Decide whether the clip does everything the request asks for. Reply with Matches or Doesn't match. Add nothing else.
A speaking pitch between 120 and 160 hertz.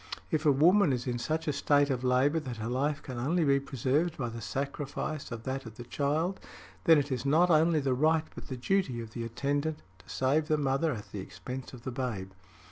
Matches